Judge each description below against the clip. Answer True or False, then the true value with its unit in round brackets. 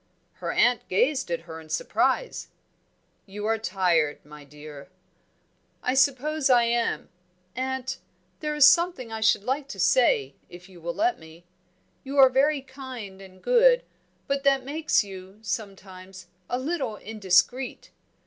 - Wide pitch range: True (6.6 semitones)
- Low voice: False (230 Hz)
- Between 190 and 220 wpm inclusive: False (145 wpm)